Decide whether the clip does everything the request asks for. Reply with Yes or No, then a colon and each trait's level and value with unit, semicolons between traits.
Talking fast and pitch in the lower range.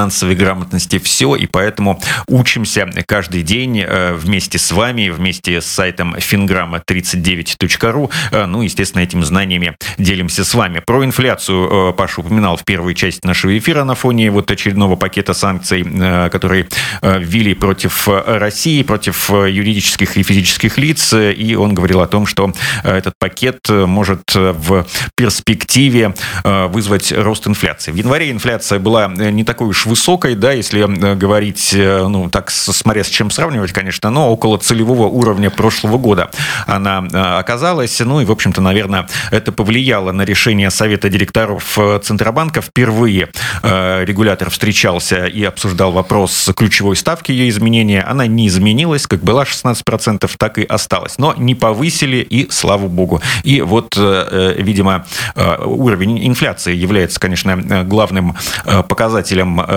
No: average, 135 wpm; low, 100 Hz